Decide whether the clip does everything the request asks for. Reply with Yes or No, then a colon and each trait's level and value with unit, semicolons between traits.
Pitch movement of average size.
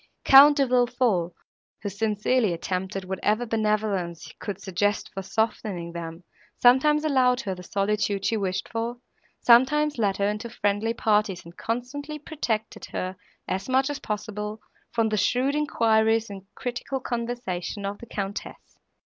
Yes: average, 3.8 semitones